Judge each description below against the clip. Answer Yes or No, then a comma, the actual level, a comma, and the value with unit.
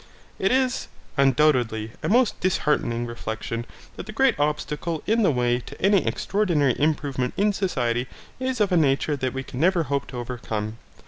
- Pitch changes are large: Yes, wide, 7.7 semitones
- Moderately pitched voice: Yes, medium, 145 Hz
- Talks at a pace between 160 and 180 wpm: Yes, average, 170 wpm